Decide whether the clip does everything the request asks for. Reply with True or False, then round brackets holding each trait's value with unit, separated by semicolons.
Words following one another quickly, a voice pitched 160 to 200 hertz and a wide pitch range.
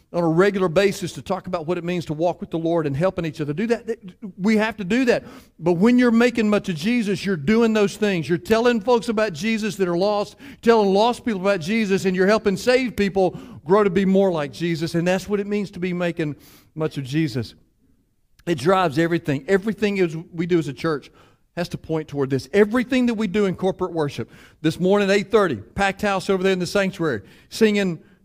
False (225 wpm; 190 Hz; 4.0 semitones)